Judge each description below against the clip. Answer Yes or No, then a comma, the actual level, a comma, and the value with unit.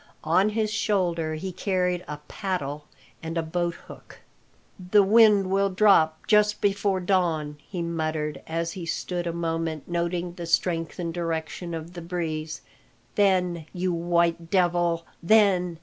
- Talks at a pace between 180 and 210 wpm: No, average, 140 wpm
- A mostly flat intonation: Yes, narrow, 2.3 semitones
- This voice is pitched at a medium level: Yes, medium, 175 Hz